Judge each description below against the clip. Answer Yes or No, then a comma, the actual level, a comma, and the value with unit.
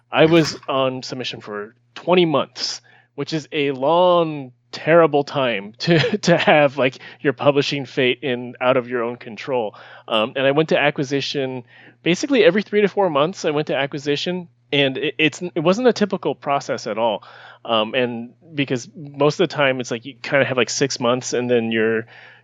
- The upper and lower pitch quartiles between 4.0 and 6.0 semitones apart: Yes, average, 4.3 semitones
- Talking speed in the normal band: Yes, average, 190 wpm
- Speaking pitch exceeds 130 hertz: Yes, medium, 140 Hz